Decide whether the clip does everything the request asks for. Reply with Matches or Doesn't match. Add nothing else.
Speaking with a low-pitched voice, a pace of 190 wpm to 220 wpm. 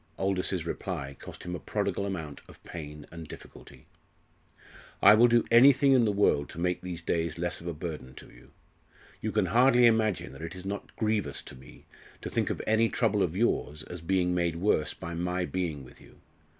Matches